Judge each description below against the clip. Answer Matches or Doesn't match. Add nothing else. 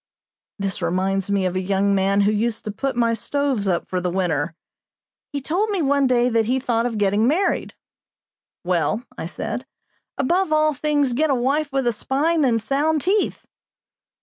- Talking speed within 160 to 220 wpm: Matches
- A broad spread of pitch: Matches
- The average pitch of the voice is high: Matches